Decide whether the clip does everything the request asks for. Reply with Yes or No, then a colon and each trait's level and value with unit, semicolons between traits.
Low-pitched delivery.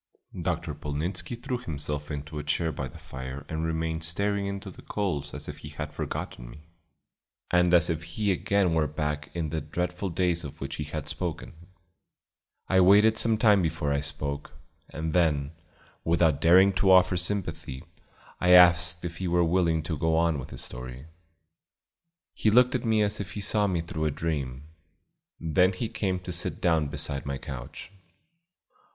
Yes: very low, 85 Hz